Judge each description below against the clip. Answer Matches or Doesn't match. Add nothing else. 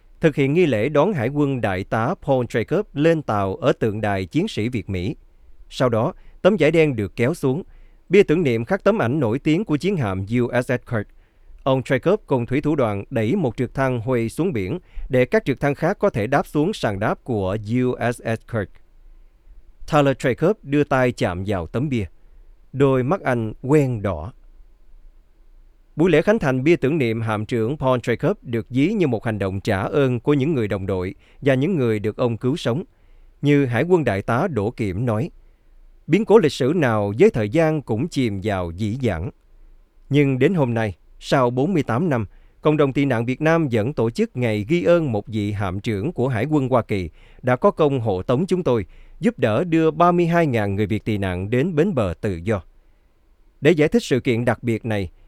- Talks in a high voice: Doesn't match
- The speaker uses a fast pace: Doesn't match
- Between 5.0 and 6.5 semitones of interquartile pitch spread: Matches